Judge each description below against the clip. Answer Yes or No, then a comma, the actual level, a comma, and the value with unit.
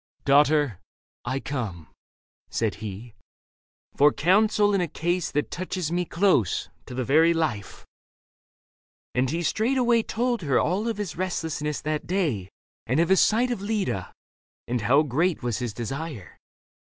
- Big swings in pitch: Yes, wide, 6.9 semitones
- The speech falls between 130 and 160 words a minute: Yes, average, 155 wpm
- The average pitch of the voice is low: No, medium, 155 Hz